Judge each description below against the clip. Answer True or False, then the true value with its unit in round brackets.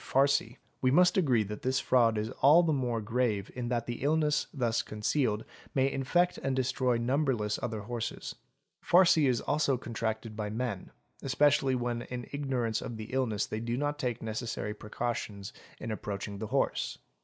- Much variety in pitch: False (3.6 semitones)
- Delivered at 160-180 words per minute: True (170 wpm)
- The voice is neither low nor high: False (120 Hz)